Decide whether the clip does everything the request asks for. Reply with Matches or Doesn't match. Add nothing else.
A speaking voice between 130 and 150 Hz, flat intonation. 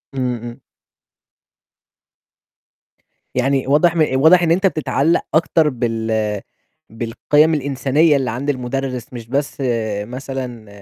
Doesn't match